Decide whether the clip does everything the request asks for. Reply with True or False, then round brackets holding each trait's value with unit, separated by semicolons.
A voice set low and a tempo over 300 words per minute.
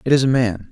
True (125 Hz; 335 wpm)